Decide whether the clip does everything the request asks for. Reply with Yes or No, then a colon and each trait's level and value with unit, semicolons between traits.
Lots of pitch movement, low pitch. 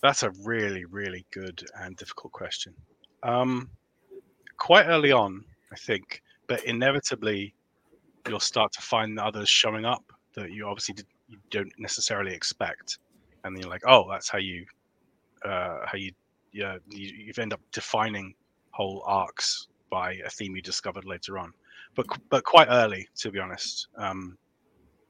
No: average, 3.6 semitones; low, 100 Hz